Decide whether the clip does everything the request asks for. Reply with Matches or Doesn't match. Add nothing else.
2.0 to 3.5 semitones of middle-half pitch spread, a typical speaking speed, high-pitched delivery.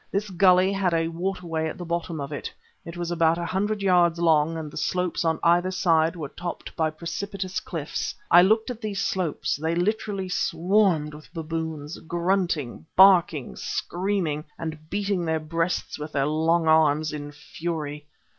Doesn't match